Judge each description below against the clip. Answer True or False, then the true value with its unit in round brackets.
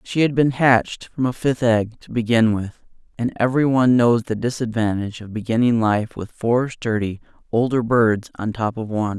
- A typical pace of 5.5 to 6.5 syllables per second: False (5.2 syllables/s)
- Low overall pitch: True (115 Hz)